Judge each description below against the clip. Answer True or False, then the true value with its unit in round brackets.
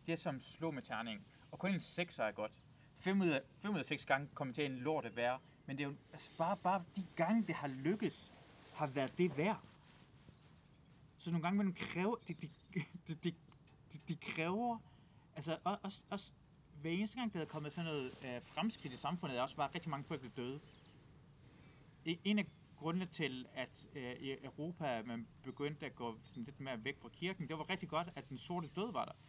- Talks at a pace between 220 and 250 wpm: False (205 wpm)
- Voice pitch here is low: False (155 Hz)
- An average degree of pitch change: True (4.0 semitones)